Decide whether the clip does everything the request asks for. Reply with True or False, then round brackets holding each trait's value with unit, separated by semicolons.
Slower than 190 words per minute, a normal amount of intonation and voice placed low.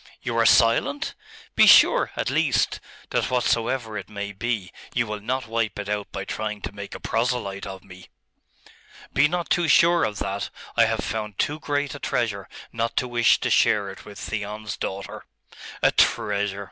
True (180 wpm; 3.4 semitones; 110 Hz)